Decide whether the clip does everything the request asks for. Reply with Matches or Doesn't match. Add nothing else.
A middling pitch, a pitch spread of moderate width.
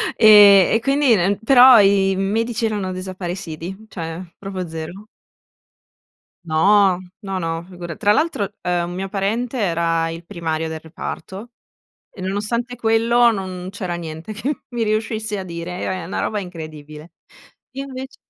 Doesn't match